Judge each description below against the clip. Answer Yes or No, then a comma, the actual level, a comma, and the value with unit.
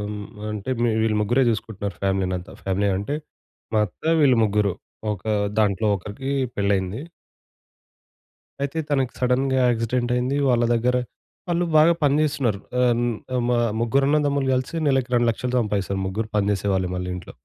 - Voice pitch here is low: Yes, low, 115 Hz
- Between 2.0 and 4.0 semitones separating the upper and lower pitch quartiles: No, average, 4.7 semitones